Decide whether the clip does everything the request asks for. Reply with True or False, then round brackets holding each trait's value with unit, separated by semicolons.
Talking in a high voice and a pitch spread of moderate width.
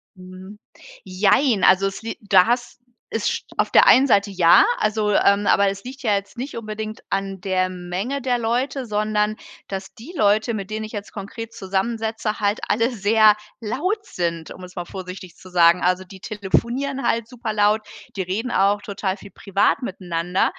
True (205 Hz; 3.1 semitones)